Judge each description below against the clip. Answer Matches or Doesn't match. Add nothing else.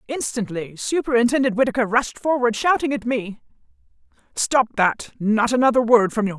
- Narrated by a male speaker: Doesn't match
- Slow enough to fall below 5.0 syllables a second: Doesn't match